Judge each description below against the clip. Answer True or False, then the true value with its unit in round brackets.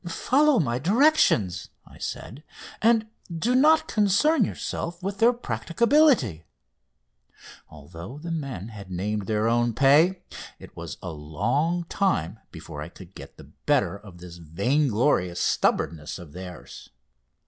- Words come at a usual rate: False (130 wpm)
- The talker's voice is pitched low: True (120 Hz)